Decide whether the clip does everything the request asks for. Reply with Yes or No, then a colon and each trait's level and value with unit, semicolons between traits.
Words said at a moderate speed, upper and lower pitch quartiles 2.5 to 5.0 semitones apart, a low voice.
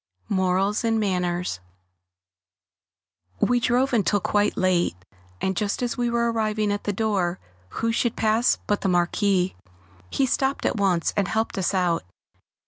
No: average, 150 wpm; average, 3.5 semitones; high, 205 Hz